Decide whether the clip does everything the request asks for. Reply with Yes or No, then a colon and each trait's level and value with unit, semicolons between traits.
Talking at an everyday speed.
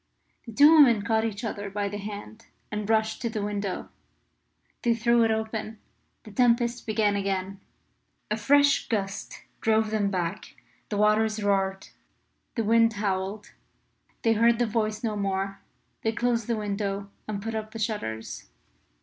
Yes: average, 155 wpm